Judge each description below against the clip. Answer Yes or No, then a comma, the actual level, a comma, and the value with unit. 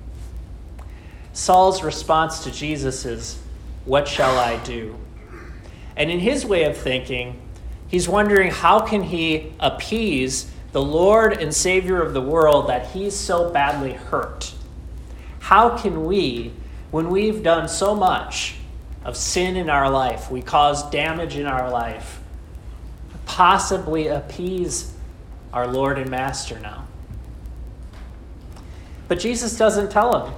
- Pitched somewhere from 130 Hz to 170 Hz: Yes, low, 135 Hz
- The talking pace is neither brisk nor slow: No, slow, 125 wpm